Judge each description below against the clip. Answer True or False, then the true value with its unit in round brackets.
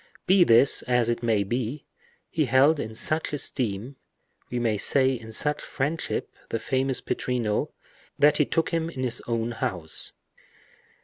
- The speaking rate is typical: True (145 wpm)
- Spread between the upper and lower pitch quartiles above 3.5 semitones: True (4.3 semitones)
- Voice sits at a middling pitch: False (125 Hz)